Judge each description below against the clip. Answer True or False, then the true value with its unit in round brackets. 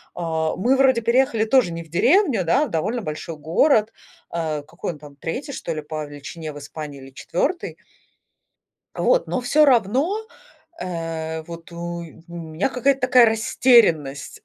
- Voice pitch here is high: False (170 Hz)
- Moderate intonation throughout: False (7.8 semitones)